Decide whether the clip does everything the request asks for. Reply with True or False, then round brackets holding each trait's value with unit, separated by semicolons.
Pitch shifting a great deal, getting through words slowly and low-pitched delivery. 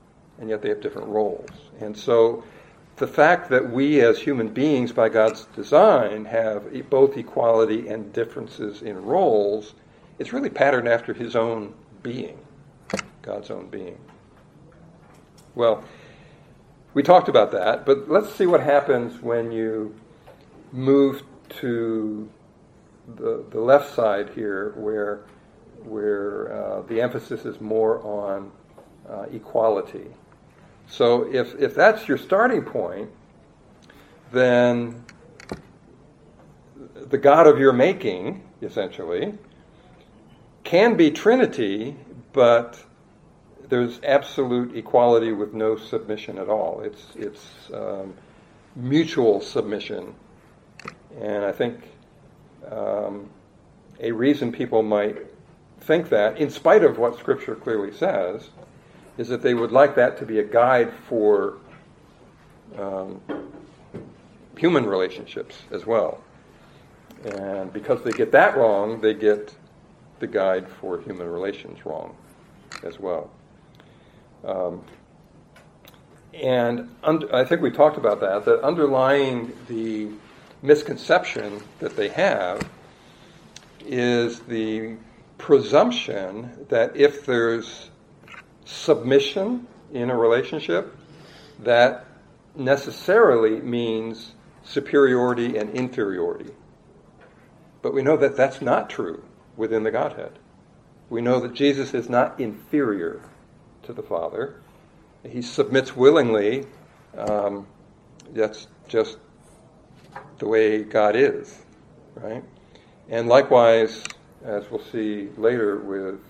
False (4.3 semitones; 110 wpm; 120 Hz)